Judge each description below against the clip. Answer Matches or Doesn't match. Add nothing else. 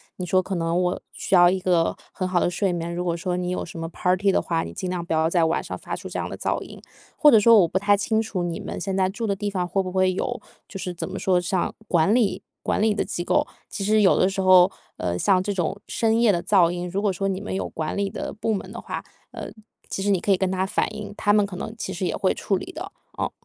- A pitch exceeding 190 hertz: Doesn't match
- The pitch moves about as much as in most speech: Doesn't match